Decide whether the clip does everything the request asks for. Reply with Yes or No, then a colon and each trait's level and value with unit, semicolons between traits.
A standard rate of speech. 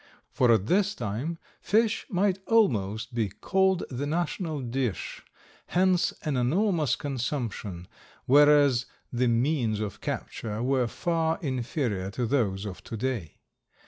No: slow, 125 wpm